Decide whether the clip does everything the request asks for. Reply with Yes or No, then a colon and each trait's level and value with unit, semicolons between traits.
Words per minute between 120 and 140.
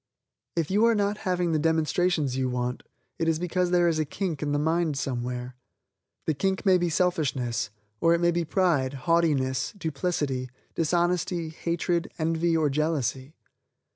No: average, 160 wpm